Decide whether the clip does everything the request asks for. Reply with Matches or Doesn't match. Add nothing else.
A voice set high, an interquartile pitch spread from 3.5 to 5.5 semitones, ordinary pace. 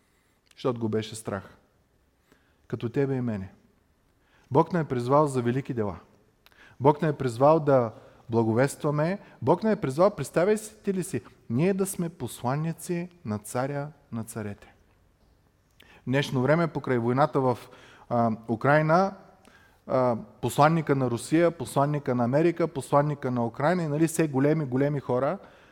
Doesn't match